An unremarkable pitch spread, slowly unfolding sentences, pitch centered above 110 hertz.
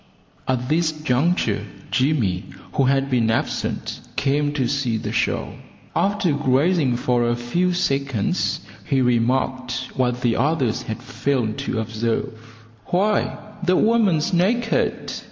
Yes: average, 4.7 semitones; slow, 125 wpm; low, 135 Hz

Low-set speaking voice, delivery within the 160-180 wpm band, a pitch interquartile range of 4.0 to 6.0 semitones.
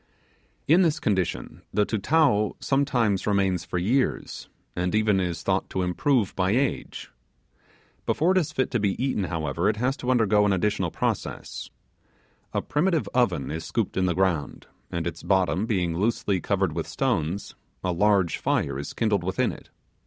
Yes: low, 100 Hz; average, 165 wpm; average, 5.2 semitones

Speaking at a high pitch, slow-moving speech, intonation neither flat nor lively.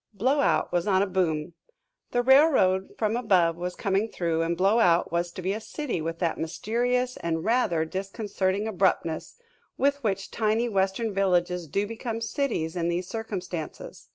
No: high, 195 Hz; average, 155 wpm; average, 4.7 semitones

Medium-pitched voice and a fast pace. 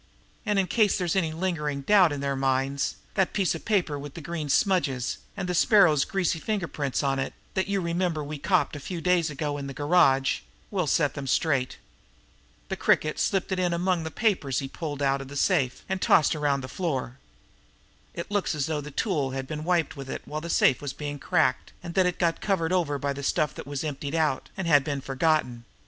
Yes: medium, 155 Hz; fast, 225 wpm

